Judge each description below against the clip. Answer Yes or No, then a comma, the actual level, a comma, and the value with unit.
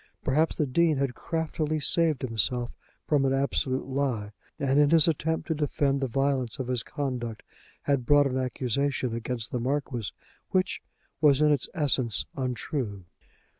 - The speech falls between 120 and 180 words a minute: Yes, average, 155 wpm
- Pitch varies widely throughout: No, average, 2.9 semitones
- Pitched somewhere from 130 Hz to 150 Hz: Yes, low, 135 Hz